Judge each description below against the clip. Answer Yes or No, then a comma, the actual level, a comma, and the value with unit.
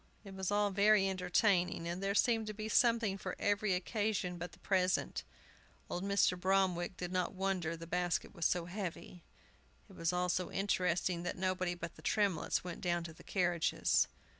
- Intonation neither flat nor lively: No, narrow, 2.2 semitones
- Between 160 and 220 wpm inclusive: Yes, average, 180 wpm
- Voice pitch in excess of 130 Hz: Yes, medium, 185 Hz